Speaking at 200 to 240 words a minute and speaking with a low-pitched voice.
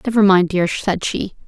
No: fast, 205 wpm; high, 190 Hz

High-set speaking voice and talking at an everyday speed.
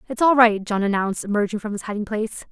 No: high, 215 Hz; fast, 240 wpm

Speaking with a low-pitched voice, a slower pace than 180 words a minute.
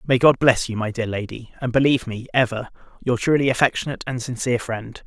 No: low, 120 Hz; average, 200 wpm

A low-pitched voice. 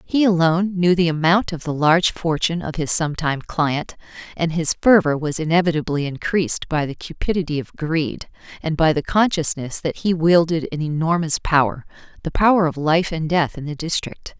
No: medium, 165 Hz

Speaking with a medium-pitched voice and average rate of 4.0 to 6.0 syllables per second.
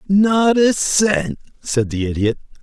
No: medium, 170 Hz; 3.5 syllables/s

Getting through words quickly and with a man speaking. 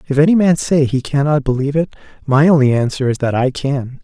Yes: fast, 225 wpm; male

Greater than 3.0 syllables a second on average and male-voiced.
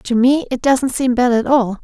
No: 4.7 syllables/s; female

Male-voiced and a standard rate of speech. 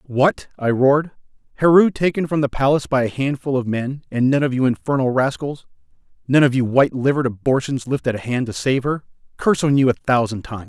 Yes: male; average, 195 wpm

